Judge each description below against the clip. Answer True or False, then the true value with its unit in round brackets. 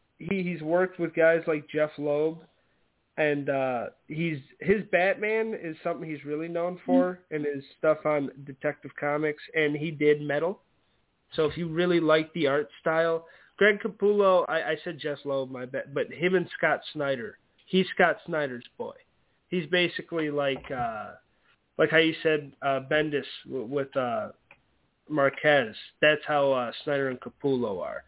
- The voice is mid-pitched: True (155 Hz)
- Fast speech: False (160 wpm)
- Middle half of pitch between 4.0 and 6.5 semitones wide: False (3.2 semitones)